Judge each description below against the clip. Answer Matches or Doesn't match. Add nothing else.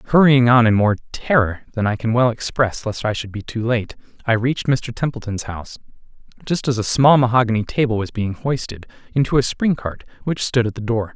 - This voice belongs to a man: Matches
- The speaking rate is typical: Doesn't match